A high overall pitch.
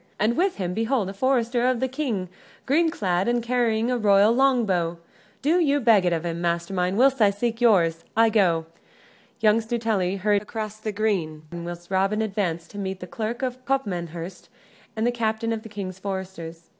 Yes: high, 210 Hz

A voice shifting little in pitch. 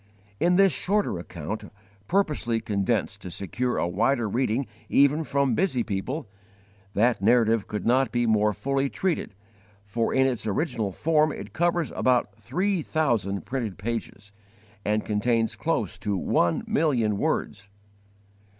No: average, 5.2 semitones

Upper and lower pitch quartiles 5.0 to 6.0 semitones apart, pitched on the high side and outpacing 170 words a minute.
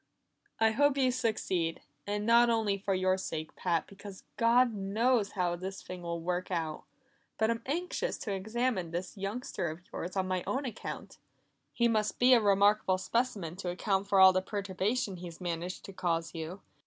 No: average, 4.1 semitones; high, 195 Hz; average, 180 wpm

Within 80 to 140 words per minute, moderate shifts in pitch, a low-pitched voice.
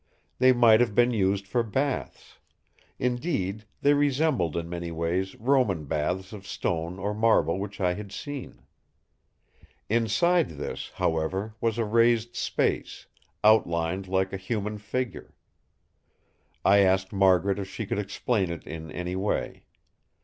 Yes: slow, 135 wpm; average, 4.2 semitones; low, 100 Hz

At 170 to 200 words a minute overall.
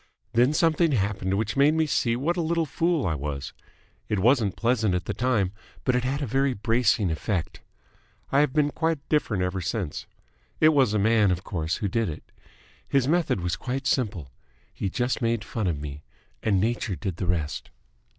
Yes: average, 190 wpm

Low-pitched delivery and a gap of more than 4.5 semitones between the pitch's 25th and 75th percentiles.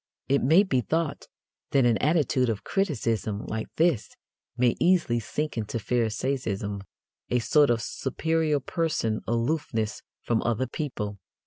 Yes: low, 125 Hz; wide, 5.4 semitones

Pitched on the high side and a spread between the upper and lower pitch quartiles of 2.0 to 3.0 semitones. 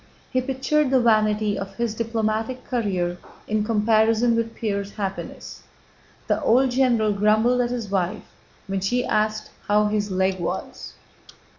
Yes: high, 215 Hz; narrow, 2.6 semitones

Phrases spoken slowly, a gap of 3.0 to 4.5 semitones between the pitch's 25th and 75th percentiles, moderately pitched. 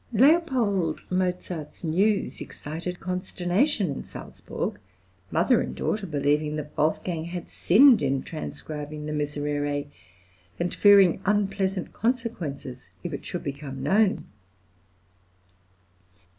No: slow, 105 wpm; average, 5.0 semitones; medium, 170 Hz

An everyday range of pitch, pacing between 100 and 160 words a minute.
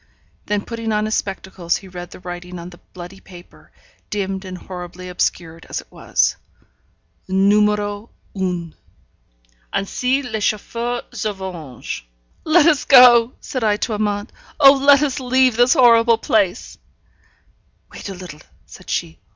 Yes: average, 4.6 semitones; average, 145 wpm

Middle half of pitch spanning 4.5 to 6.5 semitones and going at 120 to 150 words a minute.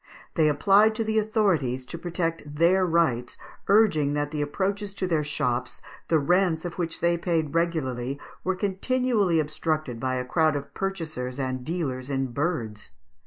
No: average, 5.1 semitones; average, 160 wpm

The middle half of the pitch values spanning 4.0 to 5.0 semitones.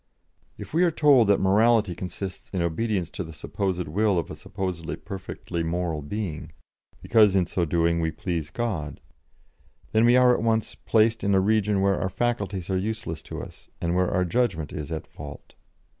Yes: average, 4.6 semitones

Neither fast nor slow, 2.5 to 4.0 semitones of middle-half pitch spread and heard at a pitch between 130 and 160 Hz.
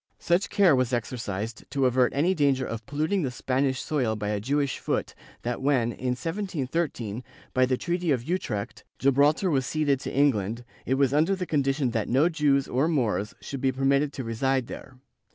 Yes: average, 190 wpm; average, 3.4 semitones; low, 135 Hz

